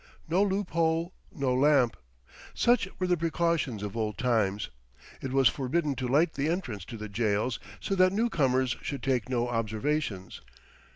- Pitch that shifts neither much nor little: No, wide, 6.4 semitones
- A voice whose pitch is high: No, low, 135 Hz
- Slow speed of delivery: No, average, 160 wpm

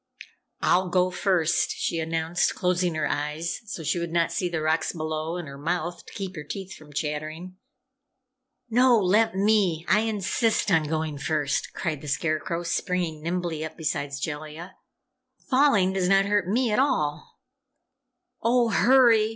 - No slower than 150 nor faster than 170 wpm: Yes, average, 155 wpm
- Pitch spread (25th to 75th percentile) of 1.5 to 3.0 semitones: No, average, 3.9 semitones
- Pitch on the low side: No, medium, 175 Hz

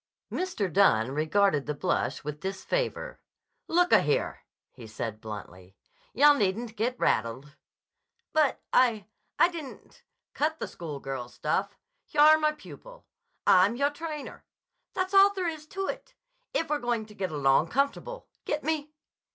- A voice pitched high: Yes, high, 230 Hz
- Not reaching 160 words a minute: Yes, slow, 135 wpm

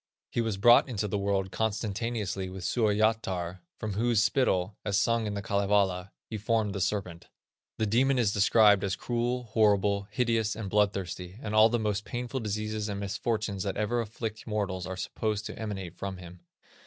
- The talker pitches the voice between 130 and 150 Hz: No, low, 105 Hz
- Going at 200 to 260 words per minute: No, average, 175 wpm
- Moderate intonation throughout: No, narrow, 2.3 semitones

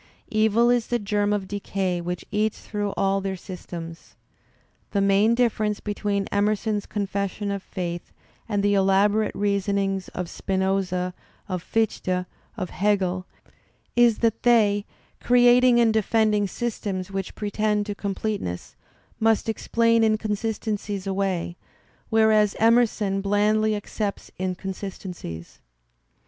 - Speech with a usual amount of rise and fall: No, narrow, 2.0 semitones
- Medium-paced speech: No, slow, 120 wpm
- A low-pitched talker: No, high, 205 Hz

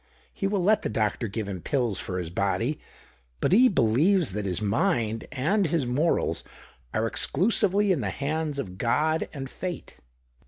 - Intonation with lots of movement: Yes, wide, 8.5 semitones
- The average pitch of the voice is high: No, low, 135 Hz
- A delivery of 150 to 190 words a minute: Yes, average, 165 wpm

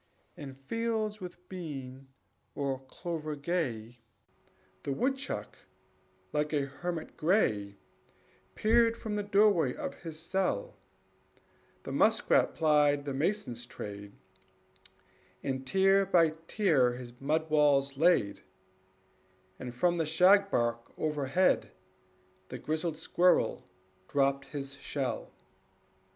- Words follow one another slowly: Yes, slow, 105 wpm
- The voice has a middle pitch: Yes, medium, 150 Hz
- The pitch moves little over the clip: No, average, 5.3 semitones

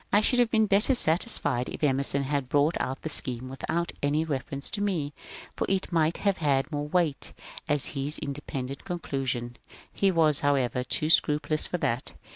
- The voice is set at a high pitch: No, medium, 150 Hz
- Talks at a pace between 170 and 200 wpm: Yes, average, 175 wpm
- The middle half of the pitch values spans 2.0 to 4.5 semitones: Yes, average, 4.0 semitones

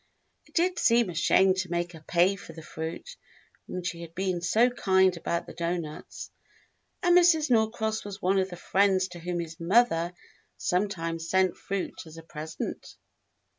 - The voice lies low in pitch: No, medium, 180 Hz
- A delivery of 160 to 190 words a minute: Yes, average, 170 wpm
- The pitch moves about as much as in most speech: Yes, average, 3.2 semitones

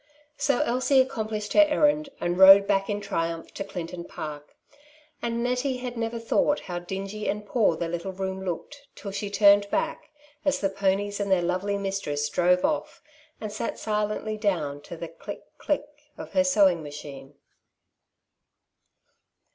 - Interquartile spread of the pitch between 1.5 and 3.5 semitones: No, average, 4.6 semitones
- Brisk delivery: No, average, 160 wpm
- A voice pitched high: Yes, high, 200 Hz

